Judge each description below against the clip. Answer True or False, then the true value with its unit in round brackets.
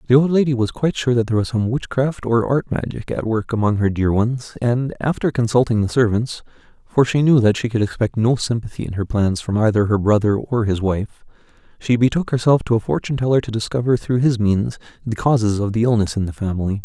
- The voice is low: True (115 Hz)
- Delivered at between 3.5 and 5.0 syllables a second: True (4.6 syllables/s)